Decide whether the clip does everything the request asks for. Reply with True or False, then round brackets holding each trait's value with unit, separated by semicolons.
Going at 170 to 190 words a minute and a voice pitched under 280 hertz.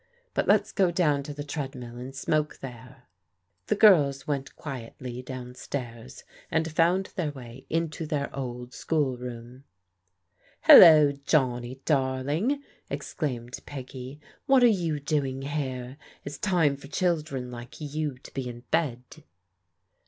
False (135 wpm; 140 Hz)